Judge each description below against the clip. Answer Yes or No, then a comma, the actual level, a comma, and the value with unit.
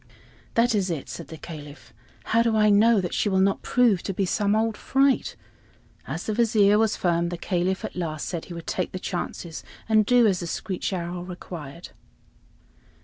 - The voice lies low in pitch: No, high, 190 Hz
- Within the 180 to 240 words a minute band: Yes, average, 195 wpm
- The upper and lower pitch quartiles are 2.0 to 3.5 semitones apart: No, average, 3.9 semitones